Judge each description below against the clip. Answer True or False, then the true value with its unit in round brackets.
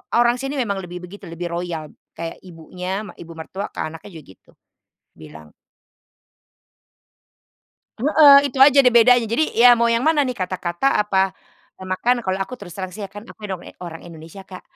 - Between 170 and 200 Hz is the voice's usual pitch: True (190 Hz)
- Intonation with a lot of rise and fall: True (5.7 semitones)